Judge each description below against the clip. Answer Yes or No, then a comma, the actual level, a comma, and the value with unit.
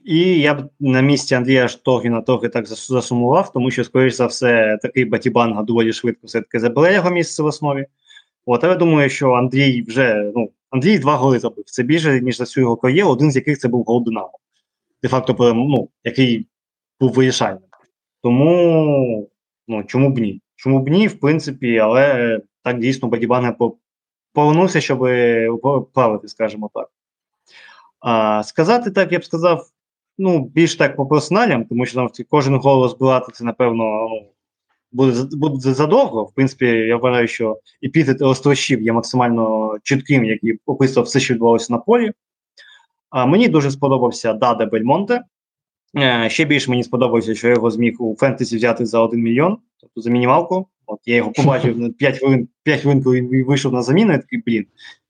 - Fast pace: Yes, fast, 165 wpm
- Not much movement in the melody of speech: No, average, 3.3 semitones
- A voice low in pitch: Yes, low, 125 Hz